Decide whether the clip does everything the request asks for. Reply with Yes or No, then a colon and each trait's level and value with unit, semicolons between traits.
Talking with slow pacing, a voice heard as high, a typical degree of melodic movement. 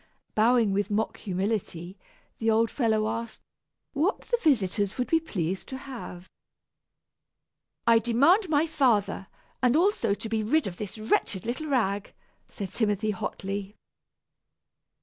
Yes: slow, 130 wpm; high, 220 Hz; average, 4.6 semitones